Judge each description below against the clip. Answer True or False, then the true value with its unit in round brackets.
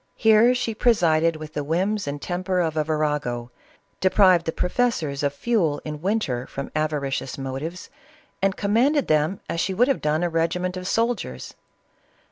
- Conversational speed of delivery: True (165 wpm)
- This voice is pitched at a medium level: True (165 Hz)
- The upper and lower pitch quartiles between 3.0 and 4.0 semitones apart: False (5.1 semitones)